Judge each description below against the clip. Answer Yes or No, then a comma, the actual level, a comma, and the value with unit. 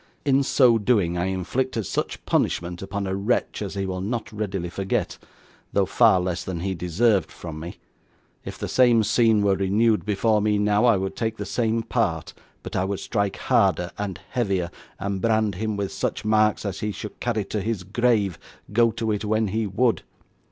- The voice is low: Yes, low, 105 Hz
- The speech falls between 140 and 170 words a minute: No, average, 190 wpm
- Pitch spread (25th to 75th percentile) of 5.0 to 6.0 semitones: No, average, 2.8 semitones